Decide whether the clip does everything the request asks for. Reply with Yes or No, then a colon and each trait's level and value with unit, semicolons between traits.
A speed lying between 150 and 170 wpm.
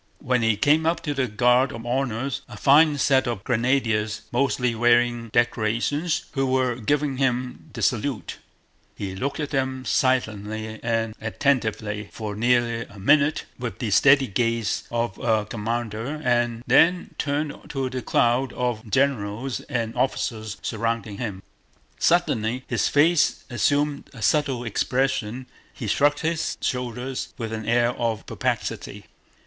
No: average, 140 wpm